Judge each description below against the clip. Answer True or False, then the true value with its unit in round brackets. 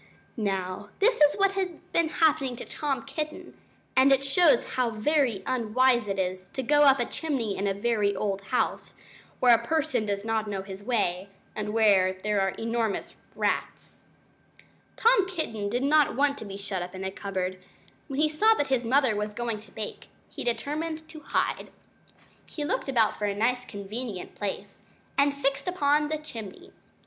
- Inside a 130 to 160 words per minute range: False (180 wpm)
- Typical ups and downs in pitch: False (6.2 semitones)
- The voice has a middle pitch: False (240 Hz)